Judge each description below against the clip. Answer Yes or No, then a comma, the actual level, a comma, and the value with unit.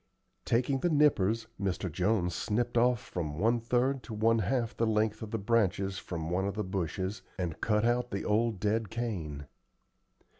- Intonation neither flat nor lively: Yes, average, 3.8 semitones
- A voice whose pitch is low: Yes, low, 110 Hz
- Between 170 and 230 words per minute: Yes, average, 175 wpm